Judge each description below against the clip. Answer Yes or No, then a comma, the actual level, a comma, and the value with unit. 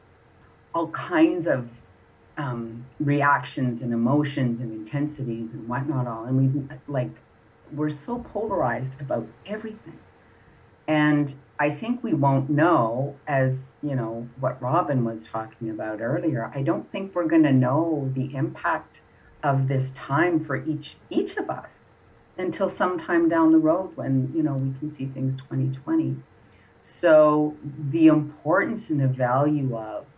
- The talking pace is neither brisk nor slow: Yes, average, 145 wpm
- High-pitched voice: No, medium, 140 Hz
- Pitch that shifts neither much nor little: Yes, average, 3.9 semitones